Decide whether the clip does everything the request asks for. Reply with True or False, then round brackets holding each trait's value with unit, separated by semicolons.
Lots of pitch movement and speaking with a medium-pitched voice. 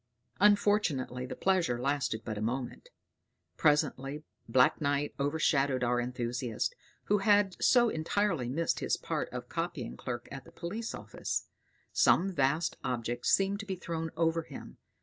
True (6.8 semitones; 145 Hz)